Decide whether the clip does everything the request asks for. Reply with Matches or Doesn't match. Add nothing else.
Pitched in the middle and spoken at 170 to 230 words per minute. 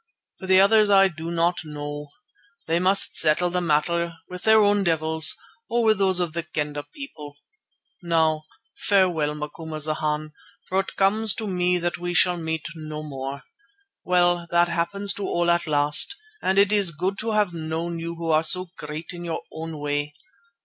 Matches